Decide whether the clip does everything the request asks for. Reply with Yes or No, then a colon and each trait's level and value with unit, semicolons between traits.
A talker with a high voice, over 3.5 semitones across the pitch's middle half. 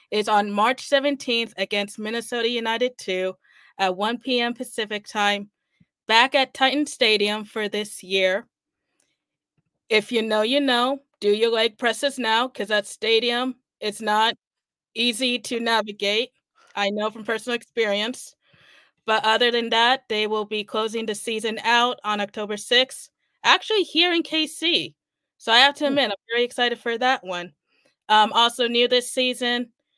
No: high, 230 Hz; average, 3.0 semitones